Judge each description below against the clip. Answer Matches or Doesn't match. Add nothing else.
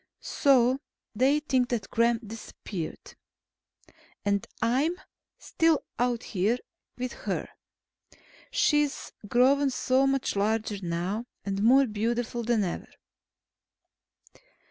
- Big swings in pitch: Doesn't match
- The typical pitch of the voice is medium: Doesn't match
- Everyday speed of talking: Doesn't match